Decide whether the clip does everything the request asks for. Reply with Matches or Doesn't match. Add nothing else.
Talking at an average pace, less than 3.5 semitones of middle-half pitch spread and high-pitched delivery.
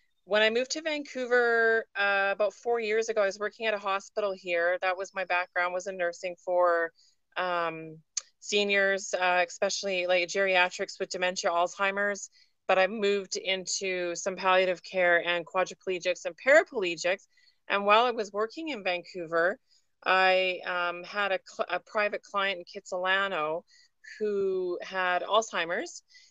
Matches